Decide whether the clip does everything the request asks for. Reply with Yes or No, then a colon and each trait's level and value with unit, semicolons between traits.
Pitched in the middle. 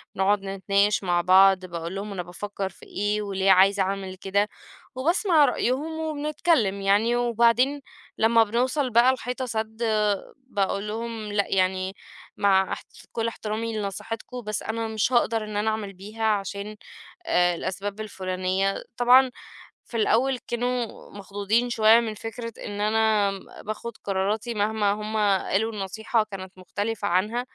No: high, 210 Hz